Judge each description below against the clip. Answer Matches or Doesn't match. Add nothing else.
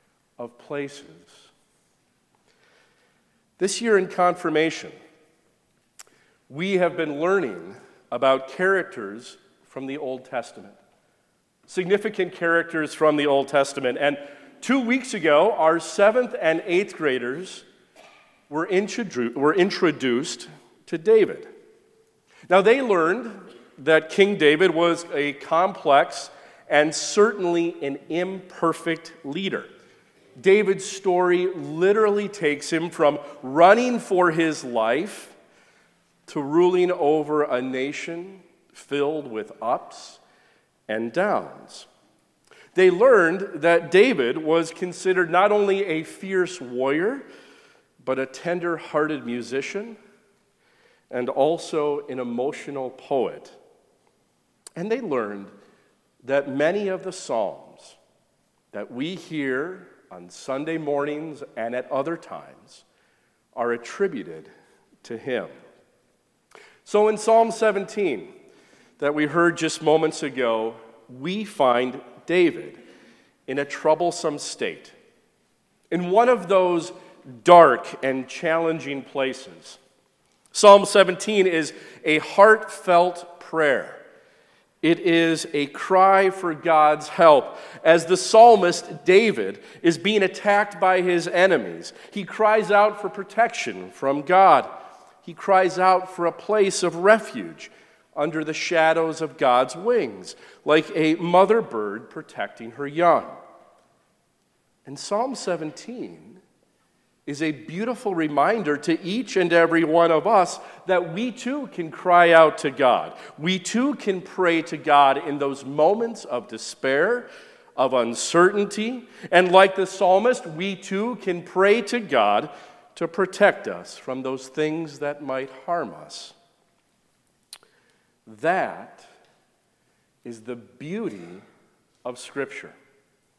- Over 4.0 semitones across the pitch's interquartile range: Matches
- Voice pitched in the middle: Matches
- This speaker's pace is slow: Matches